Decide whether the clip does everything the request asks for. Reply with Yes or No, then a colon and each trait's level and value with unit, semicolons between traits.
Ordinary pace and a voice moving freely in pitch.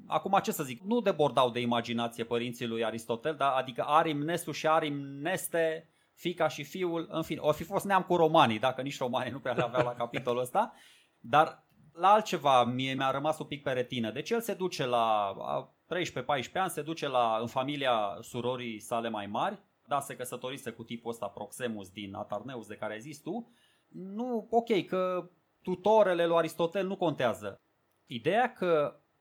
No: fast, 180 wpm; wide, 6.0 semitones